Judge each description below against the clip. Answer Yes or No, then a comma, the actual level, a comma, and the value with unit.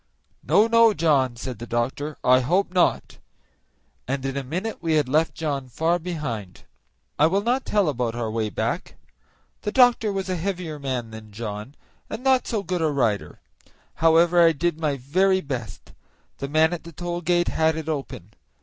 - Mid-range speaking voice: Yes, medium, 155 Hz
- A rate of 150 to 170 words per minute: No, average, 180 wpm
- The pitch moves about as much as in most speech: No, wide, 5.8 semitones